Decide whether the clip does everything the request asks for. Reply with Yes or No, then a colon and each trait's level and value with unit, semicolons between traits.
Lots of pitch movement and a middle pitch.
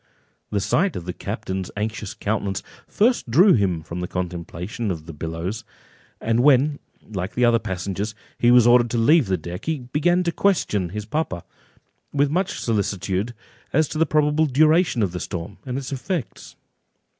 No: wide, 7.9 semitones; low, 115 Hz